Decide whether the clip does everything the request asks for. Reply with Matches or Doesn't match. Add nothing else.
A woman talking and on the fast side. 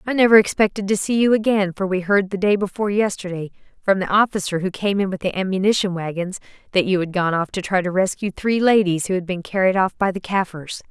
Matches